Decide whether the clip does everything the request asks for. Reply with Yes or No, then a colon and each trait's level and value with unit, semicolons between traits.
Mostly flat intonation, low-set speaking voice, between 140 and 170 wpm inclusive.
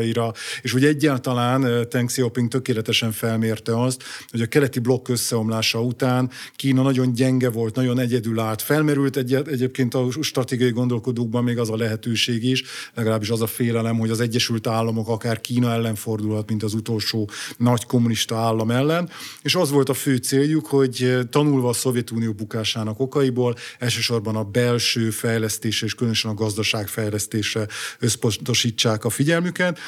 Yes: narrow, 2.3 semitones; low, 120 Hz; average, 150 wpm